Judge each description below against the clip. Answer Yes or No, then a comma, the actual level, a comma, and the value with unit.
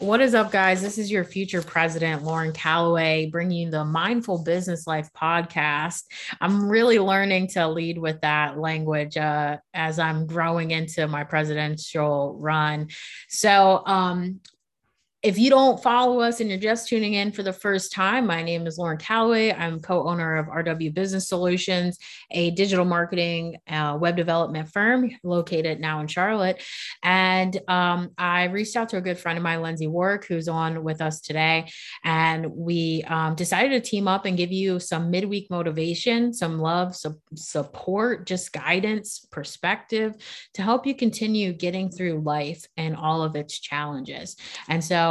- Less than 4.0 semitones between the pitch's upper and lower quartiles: Yes, average, 3.2 semitones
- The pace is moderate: Yes, average, 170 wpm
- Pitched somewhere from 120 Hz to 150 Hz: No, medium, 170 Hz